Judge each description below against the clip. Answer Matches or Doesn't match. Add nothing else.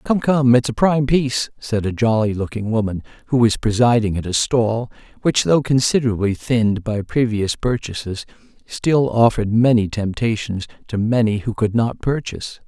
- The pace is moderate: Matches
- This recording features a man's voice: Matches